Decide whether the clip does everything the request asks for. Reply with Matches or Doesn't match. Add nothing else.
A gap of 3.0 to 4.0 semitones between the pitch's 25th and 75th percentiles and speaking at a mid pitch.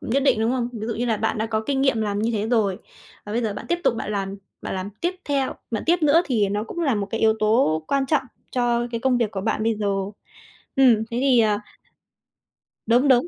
Doesn't match